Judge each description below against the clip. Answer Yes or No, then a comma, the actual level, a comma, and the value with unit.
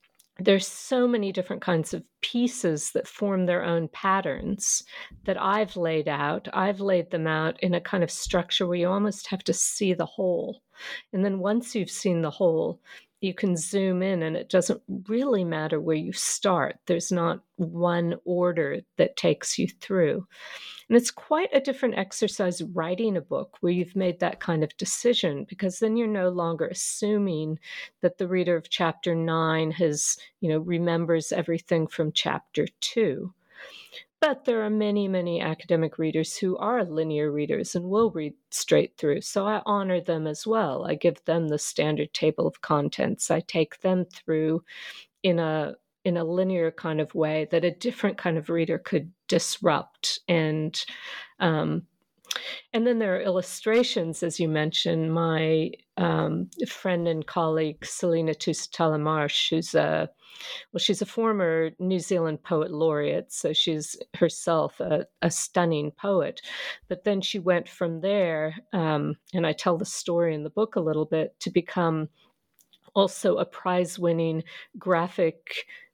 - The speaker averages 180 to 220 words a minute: No, average, 160 wpm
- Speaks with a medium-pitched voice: Yes, medium, 180 Hz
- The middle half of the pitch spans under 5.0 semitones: Yes, average, 4.0 semitones